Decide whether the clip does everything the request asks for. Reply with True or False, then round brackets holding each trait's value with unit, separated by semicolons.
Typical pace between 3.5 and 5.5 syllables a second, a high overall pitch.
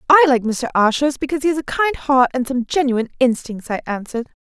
False (6.2 syllables/s; 265 Hz)